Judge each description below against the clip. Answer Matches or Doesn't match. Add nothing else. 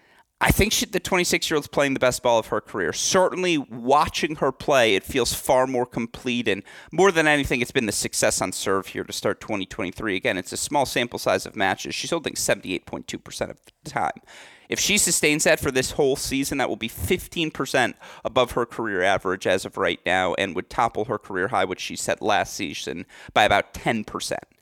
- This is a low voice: Doesn't match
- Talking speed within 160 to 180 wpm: Doesn't match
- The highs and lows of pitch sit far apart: Matches